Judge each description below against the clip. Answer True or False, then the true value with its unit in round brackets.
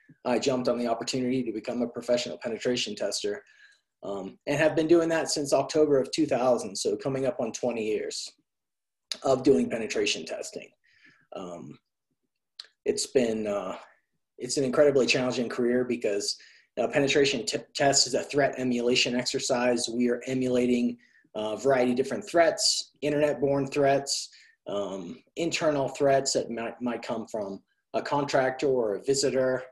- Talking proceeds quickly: False (150 wpm)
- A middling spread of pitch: True (3.8 semitones)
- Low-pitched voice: True (130 Hz)